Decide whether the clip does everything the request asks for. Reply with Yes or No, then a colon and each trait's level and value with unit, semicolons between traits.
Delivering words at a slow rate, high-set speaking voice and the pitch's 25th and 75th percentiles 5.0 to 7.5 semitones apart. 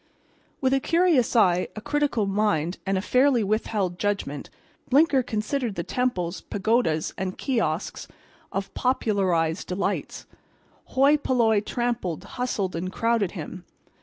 Yes: slow, 125 wpm; high, 215 Hz; average, 5.3 semitones